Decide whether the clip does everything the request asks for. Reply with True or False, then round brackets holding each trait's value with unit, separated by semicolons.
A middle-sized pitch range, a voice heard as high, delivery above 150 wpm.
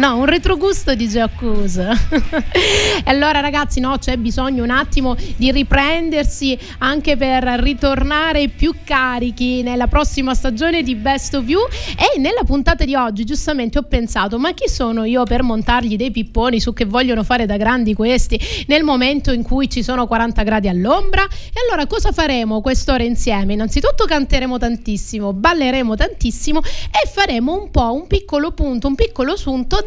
True (3.7 semitones; 260 Hz; 165 wpm)